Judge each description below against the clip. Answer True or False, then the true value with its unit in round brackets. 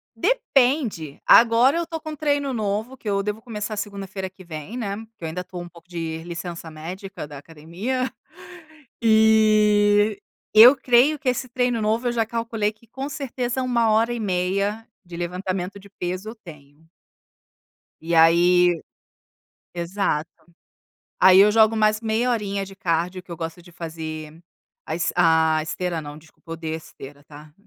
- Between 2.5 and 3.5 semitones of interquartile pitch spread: False (5.2 semitones)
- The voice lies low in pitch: False (200 Hz)